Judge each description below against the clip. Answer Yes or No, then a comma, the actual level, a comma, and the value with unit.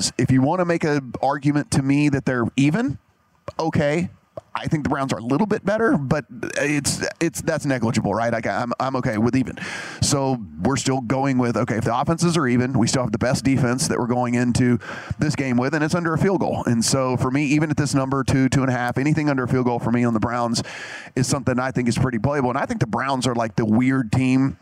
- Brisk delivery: Yes, fast, 255 wpm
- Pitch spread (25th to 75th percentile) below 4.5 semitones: Yes, average, 2.9 semitones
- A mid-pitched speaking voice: No, low, 130 Hz